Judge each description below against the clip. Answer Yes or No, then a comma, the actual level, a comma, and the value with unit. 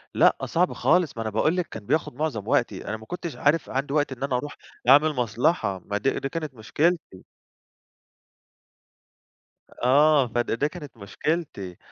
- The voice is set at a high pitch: No, medium, 140 Hz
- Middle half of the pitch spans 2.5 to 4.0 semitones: No, wide, 5.5 semitones